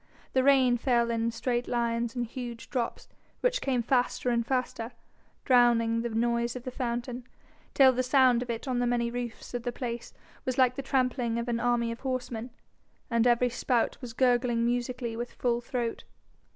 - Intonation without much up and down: Yes, narrow, 1.3 semitones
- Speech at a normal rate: Yes, average, 180 wpm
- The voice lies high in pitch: Yes, high, 240 Hz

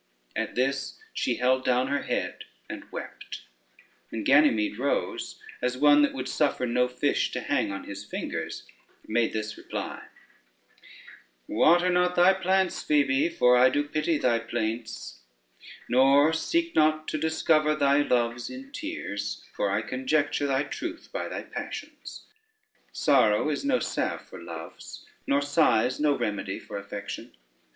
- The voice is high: No, low, 135 Hz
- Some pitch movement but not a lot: Yes, average, 4.5 semitones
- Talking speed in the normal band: Yes, average, 145 wpm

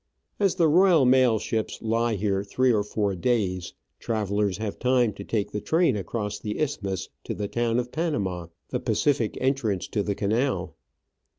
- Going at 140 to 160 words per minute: No, average, 170 wpm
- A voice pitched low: Yes, low, 110 Hz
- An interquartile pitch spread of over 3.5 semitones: Yes, average, 4.1 semitones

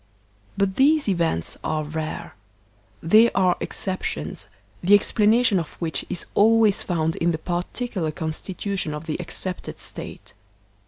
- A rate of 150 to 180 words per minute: No, average, 140 wpm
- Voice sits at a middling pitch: Yes, medium, 180 Hz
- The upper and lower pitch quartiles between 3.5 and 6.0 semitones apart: Yes, average, 4.3 semitones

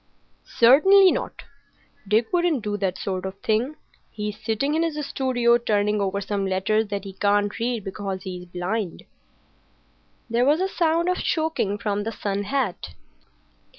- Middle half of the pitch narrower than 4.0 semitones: No, wide, 5.4 semitones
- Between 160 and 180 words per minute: No, average, 150 wpm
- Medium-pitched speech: No, high, 215 Hz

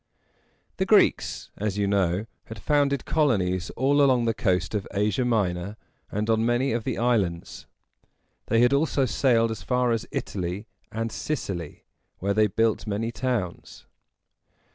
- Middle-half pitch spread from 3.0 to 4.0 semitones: Yes, average, 3.7 semitones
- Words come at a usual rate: Yes, average, 145 wpm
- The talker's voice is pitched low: Yes, low, 110 Hz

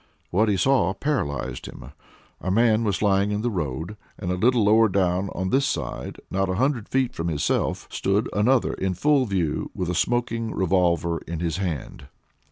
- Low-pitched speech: Yes, very low, 95 Hz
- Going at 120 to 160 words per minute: No, average, 180 wpm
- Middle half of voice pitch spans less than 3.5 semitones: No, average, 4.6 semitones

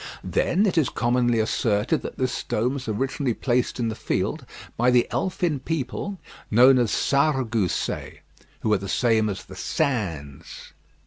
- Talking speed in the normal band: Yes, average, 150 wpm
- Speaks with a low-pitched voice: Yes, low, 120 Hz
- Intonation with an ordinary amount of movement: Yes, average, 3.8 semitones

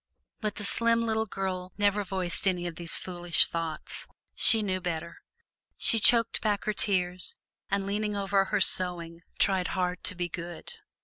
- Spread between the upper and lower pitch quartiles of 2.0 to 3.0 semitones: Yes, average, 2.7 semitones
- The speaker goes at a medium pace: Yes, average, 165 wpm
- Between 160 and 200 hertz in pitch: Yes, high, 190 Hz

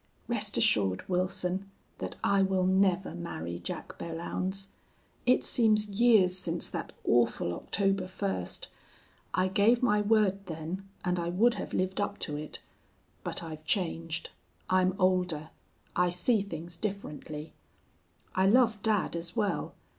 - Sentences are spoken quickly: No, slow, 135 wpm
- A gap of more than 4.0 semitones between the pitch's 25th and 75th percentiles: No, average, 3.2 semitones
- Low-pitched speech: No, medium, 185 Hz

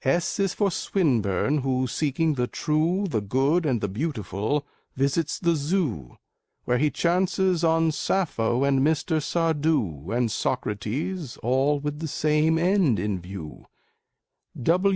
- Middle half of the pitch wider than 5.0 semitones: Yes, wide, 5.5 semitones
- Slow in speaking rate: Yes, slow, 130 wpm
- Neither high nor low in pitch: Yes, medium, 145 Hz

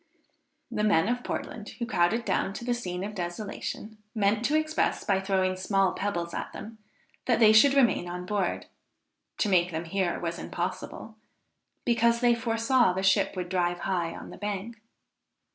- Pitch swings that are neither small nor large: Yes, average, 4.2 semitones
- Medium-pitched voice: No, high, 205 Hz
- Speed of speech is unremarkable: Yes, average, 170 wpm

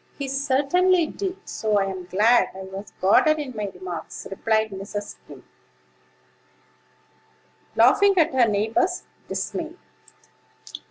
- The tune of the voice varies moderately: No, wide, 7.9 semitones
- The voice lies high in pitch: Yes, high, 225 Hz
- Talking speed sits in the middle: No, slow, 110 wpm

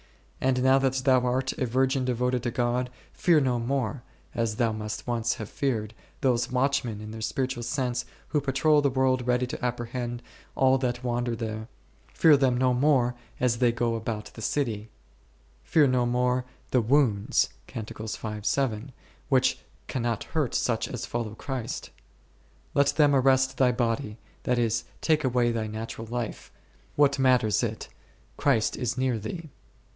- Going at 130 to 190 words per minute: Yes, average, 160 wpm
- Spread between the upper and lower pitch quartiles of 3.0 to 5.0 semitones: No, narrow, 2.4 semitones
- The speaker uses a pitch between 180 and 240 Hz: No, low, 125 Hz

